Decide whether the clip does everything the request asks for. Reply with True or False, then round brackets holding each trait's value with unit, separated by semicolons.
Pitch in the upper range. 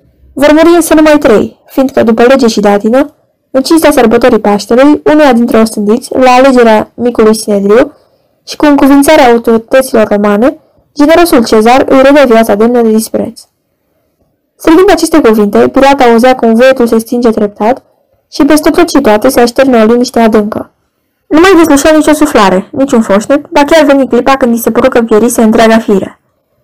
True (250 Hz)